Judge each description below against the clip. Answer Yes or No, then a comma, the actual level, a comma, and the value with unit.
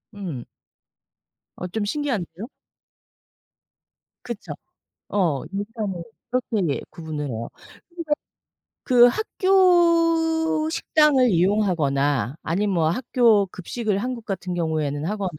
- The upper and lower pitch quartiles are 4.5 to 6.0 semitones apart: No, wide, 7.3 semitones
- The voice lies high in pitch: Yes, high, 205 Hz